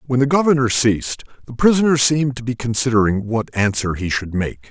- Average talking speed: Yes, average, 190 wpm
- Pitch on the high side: No, low, 120 Hz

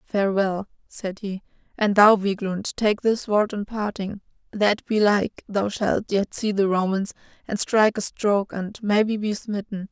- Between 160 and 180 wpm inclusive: Yes, average, 165 wpm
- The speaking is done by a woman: Yes, female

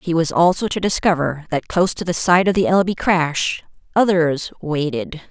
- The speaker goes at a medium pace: Yes, average, 190 wpm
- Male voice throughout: No, female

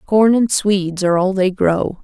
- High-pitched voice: Yes, high, 195 Hz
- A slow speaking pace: No, fast, 205 wpm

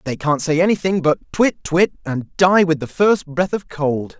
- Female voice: No, male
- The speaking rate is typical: No, fast, 215 wpm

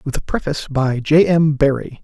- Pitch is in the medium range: Yes, medium, 145 Hz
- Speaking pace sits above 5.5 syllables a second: No, 5.3 syllables/s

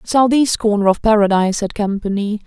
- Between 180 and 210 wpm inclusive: No, average, 145 wpm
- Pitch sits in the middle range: No, high, 210 Hz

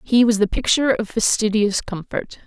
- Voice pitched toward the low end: No, high, 220 Hz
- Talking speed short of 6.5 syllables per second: Yes, 5.2 syllables/s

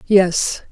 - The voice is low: No, high, 190 Hz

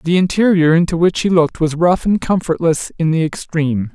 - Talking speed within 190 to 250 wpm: Yes, average, 200 wpm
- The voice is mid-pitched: Yes, medium, 165 Hz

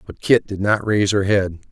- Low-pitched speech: Yes, low, 100 Hz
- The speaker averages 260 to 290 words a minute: No, fast, 245 wpm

